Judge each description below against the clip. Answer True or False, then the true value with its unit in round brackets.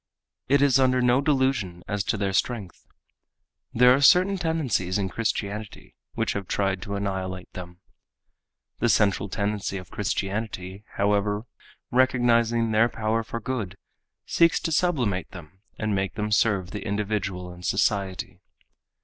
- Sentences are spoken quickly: False (140 wpm)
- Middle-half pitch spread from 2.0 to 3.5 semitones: False (4.1 semitones)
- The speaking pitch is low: True (105 Hz)